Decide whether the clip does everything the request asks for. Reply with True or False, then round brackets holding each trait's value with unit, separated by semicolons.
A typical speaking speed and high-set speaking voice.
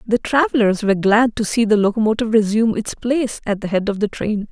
False (225 wpm; 220 Hz)